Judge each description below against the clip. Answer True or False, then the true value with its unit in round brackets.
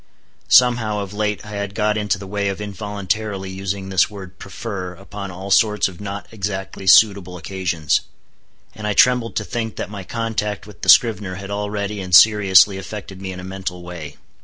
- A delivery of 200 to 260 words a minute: False (185 wpm)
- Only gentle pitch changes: True (1.8 semitones)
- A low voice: True (100 Hz)